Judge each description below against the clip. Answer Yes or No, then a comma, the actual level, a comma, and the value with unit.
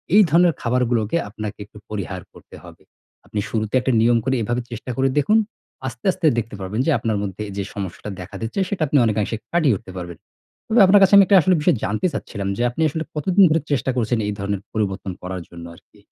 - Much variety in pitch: Yes, wide, 7.0 semitones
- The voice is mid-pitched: No, low, 115 Hz